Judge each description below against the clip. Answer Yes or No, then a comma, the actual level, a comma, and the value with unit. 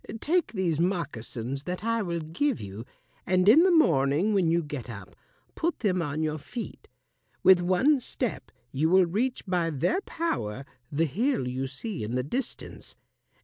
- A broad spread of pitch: Yes, wide, 8.2 semitones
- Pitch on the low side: No, medium, 170 Hz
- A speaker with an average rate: Yes, average, 165 wpm